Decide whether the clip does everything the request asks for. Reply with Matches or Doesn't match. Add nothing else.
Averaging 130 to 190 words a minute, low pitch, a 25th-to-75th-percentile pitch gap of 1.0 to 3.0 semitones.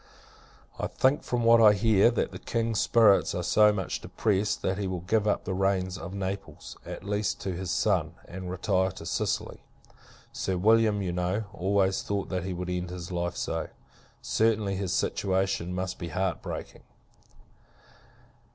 Matches